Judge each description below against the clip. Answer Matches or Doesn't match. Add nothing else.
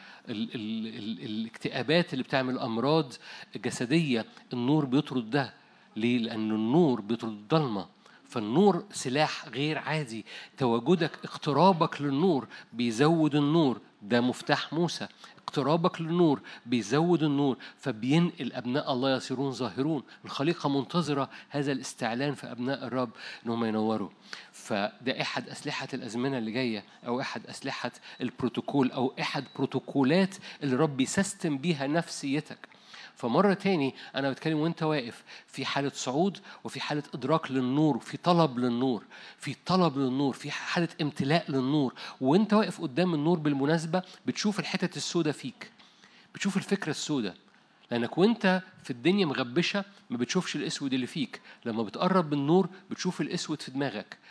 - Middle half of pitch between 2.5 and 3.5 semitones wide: Doesn't match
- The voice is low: Doesn't match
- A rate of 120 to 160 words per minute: Matches